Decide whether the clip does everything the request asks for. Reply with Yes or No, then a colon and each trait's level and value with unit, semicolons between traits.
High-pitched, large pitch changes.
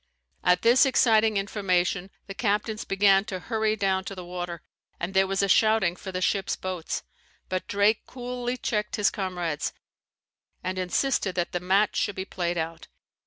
No: high, 195 Hz; average, 2.9 semitones